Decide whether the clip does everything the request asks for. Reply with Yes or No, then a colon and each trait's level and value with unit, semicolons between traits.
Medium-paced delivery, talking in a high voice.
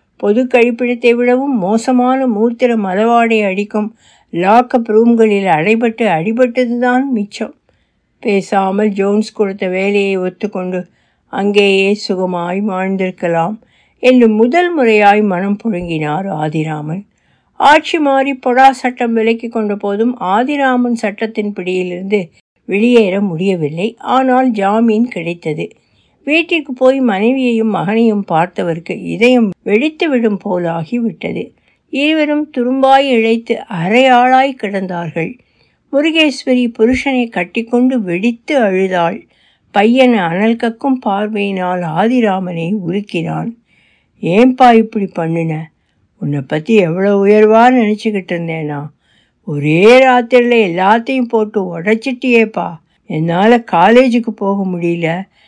Yes: average, 90 wpm; high, 215 Hz